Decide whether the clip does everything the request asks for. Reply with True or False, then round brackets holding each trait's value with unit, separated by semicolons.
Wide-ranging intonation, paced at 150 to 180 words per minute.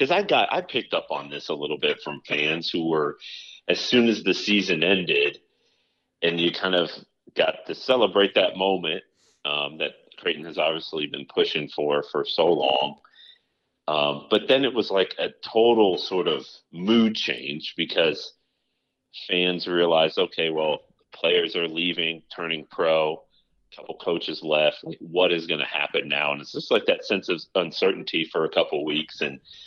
True (6.5 semitones; 175 wpm)